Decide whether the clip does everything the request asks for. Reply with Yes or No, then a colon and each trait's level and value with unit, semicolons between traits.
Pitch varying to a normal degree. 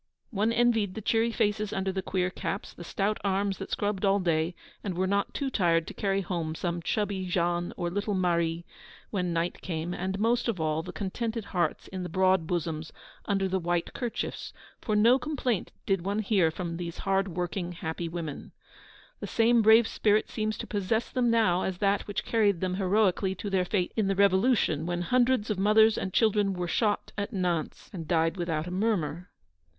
Yes: average, 3.3 semitones